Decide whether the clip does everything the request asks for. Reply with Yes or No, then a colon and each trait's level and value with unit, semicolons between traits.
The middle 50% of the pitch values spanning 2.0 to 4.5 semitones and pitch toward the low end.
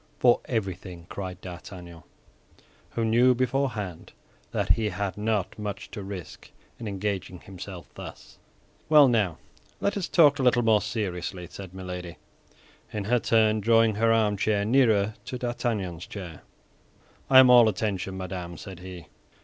Yes: average, 3.8 semitones; low, 105 Hz